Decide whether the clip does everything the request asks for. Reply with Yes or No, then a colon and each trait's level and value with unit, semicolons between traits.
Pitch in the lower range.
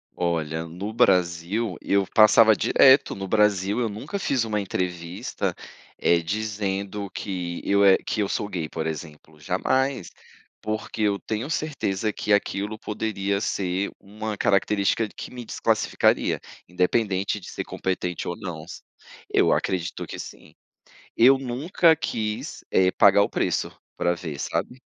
Yes: low, 100 Hz